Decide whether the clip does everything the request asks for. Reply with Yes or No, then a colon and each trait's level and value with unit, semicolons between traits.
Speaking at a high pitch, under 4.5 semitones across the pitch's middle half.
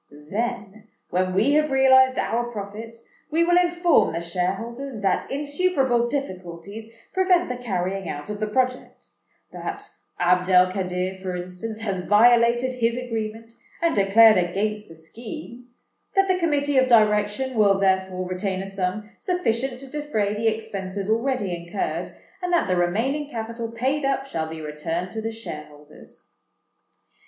No: high, 220 Hz; wide, 5.6 semitones